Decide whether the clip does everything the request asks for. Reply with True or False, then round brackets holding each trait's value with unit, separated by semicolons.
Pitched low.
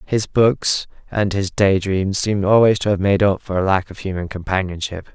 True (95 Hz)